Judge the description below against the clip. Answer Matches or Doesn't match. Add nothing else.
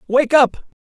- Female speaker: Doesn't match